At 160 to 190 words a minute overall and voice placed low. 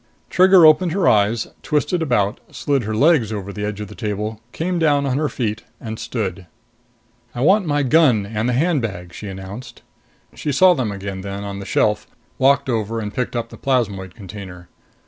Yes: average, 185 wpm; low, 115 Hz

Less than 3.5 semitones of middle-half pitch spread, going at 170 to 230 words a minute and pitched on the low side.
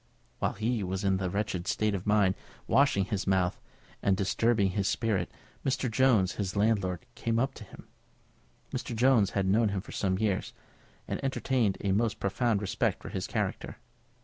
Yes: average, 3.0 semitones; average, 175 wpm; low, 105 Hz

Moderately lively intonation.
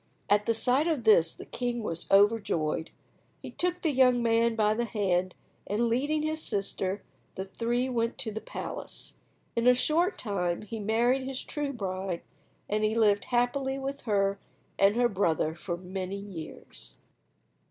Yes: average, 4.1 semitones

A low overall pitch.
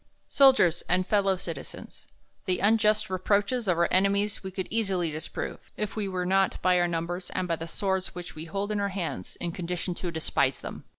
No: medium, 185 Hz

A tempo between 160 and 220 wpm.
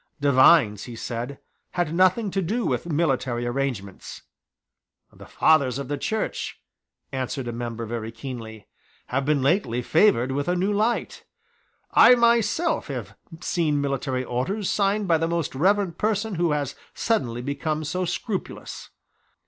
No: average, 140 wpm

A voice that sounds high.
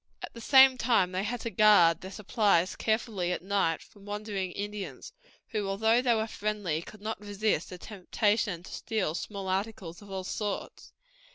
Yes: high, 205 Hz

